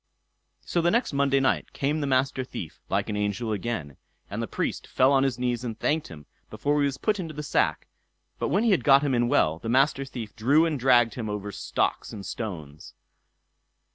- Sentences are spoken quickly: Yes, fast, 210 wpm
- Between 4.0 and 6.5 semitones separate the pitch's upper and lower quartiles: Yes, average, 4.7 semitones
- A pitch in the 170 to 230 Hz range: No, low, 130 Hz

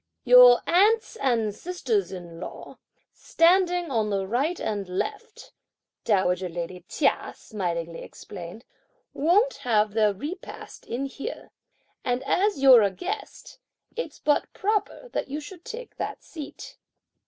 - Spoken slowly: Yes, slow, 130 wpm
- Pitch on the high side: Yes, very high, 255 Hz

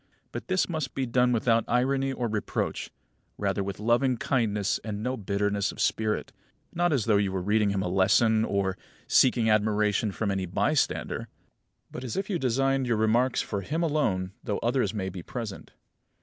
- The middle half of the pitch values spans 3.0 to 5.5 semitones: Yes, average, 4.1 semitones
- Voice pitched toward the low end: Yes, low, 110 Hz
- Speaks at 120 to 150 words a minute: No, average, 180 wpm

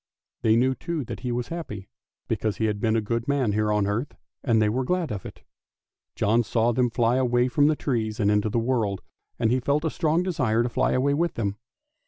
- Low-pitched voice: Yes, low, 120 Hz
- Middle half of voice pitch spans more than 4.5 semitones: No, average, 3.3 semitones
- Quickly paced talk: Yes, fast, 230 wpm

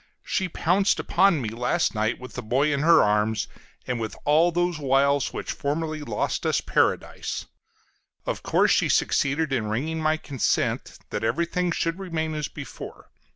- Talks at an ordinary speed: Yes, average, 160 wpm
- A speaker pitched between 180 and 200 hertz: No, medium, 150 Hz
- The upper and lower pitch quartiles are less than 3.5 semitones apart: No, average, 5.2 semitones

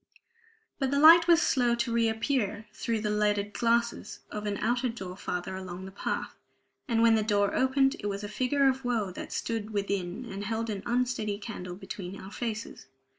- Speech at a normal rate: Yes, average, 185 wpm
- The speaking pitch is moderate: No, high, 220 Hz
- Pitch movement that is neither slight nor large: Yes, average, 3.2 semitones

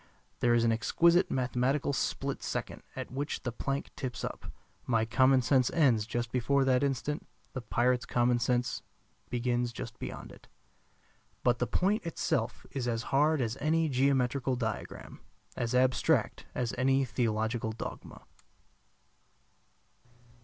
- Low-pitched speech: Yes, low, 125 Hz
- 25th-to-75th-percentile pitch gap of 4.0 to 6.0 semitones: No, narrow, 2.4 semitones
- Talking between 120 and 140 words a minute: Yes, slow, 135 wpm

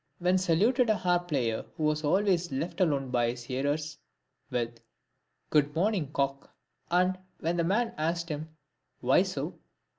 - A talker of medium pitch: Yes, medium, 160 Hz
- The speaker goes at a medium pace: Yes, average, 160 wpm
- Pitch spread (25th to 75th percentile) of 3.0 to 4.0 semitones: No, average, 4.5 semitones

